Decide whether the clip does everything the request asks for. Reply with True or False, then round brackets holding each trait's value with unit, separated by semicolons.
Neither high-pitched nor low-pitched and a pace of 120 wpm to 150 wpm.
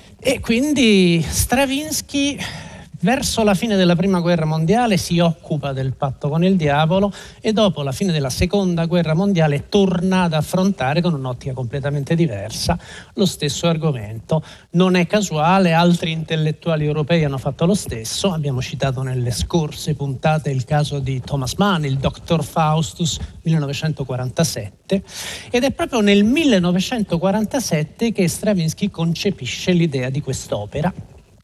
True (165 Hz; 135 wpm)